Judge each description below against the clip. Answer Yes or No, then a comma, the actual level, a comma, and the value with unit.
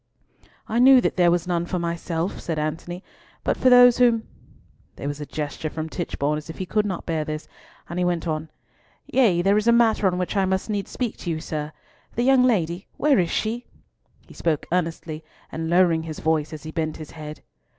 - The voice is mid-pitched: Yes, medium, 175 Hz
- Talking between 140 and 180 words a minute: No, fast, 205 wpm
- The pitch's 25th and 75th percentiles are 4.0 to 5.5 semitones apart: Yes, average, 4.7 semitones